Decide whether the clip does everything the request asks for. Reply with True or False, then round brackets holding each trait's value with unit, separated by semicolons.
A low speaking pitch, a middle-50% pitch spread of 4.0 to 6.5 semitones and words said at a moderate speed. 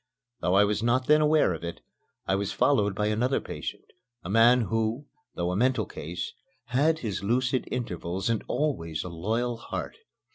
True (110 Hz; 4.8 semitones; 175 wpm)